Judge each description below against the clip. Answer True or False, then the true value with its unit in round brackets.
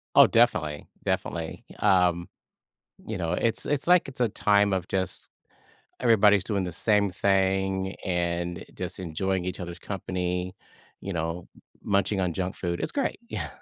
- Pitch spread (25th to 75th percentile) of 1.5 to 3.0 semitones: True (2.5 semitones)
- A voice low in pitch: True (95 Hz)